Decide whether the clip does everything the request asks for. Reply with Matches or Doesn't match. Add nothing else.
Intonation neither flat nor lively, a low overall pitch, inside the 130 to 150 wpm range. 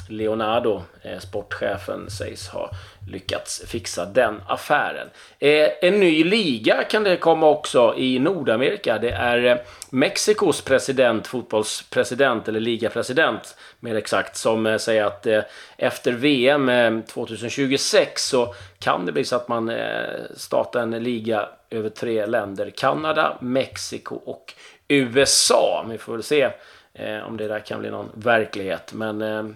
Matches